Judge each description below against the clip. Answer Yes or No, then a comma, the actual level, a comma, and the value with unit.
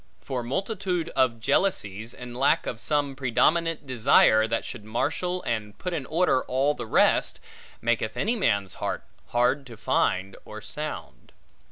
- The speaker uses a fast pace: No, average, 150 wpm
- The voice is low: Yes, low, 125 Hz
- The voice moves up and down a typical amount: No, wide, 6.0 semitones